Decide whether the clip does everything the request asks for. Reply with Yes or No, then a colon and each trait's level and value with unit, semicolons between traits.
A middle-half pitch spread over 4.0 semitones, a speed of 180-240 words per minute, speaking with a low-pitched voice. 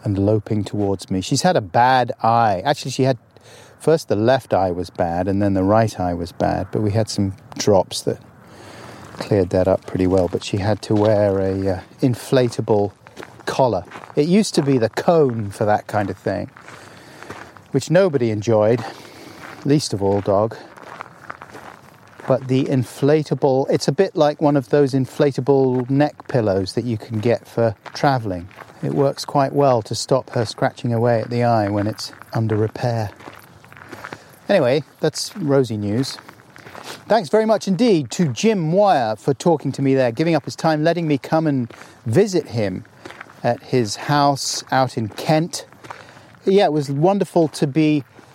No: average, 5.3 semitones; average, 170 wpm; low, 125 Hz